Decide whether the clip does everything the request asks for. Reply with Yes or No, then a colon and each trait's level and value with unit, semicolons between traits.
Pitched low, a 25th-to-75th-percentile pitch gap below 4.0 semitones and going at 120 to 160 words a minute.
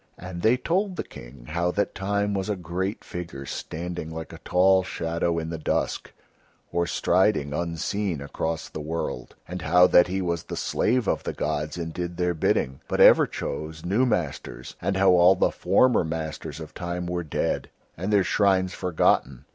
No: very low, 90 Hz; average, 2.9 semitones; average, 180 wpm